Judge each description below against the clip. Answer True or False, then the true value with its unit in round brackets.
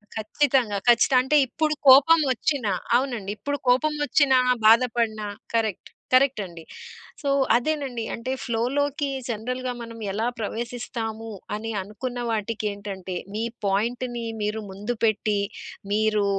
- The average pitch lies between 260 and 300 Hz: False (230 Hz)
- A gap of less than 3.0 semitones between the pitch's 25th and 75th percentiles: False (3.3 semitones)